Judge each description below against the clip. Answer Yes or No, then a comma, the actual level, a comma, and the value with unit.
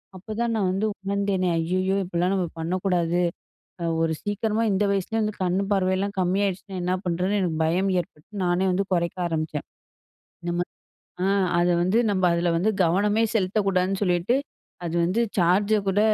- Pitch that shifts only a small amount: Yes, narrow, 2.2 semitones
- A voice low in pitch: No, medium, 185 Hz